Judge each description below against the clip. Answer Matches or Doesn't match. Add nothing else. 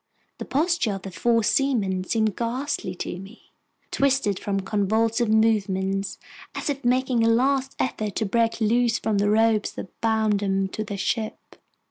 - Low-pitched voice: Doesn't match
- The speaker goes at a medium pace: Matches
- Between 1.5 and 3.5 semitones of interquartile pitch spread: Matches